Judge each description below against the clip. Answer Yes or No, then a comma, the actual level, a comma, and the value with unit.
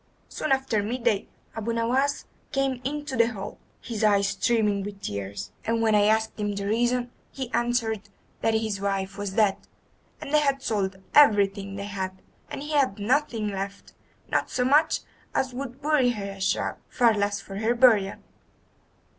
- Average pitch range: Yes, average, 4.0 semitones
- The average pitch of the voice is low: No, high, 220 Hz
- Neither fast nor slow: Yes, average, 170 wpm